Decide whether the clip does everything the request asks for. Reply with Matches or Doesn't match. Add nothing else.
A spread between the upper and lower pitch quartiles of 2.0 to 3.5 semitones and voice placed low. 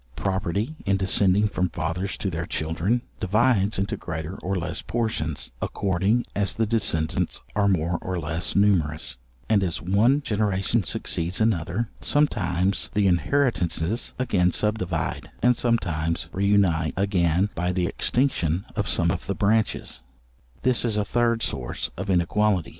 Doesn't match